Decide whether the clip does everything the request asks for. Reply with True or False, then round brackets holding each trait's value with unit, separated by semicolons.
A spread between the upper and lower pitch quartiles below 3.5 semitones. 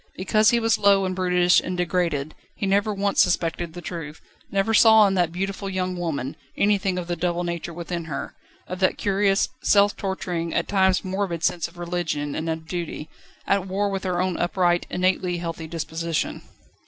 True (2.4 semitones)